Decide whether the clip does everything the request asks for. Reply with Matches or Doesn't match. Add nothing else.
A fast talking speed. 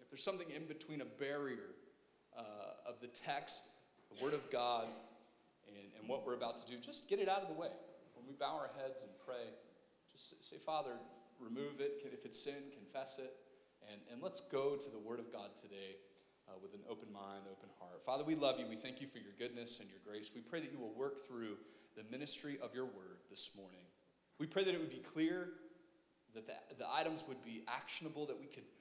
Matches